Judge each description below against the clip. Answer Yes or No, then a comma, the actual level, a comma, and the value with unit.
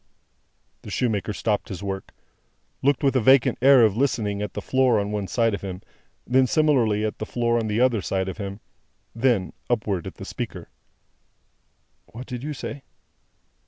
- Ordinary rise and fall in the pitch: Yes, average, 4.0 semitones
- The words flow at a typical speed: Yes, average, 175 wpm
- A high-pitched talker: No, low, 115 Hz